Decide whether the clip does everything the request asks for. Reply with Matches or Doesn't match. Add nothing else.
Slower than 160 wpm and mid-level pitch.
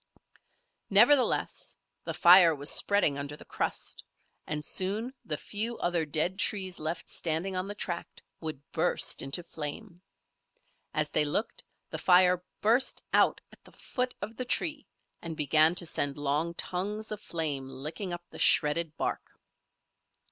Matches